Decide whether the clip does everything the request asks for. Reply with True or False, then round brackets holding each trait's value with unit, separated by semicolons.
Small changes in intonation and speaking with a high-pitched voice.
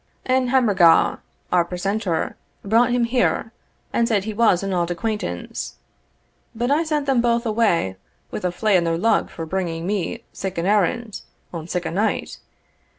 False (5.0 semitones; 205 Hz)